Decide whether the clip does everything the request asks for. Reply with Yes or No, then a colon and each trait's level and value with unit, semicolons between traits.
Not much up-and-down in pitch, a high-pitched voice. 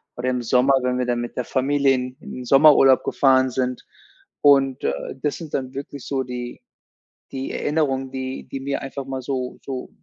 No: narrow, 1.4 semitones; low, 130 Hz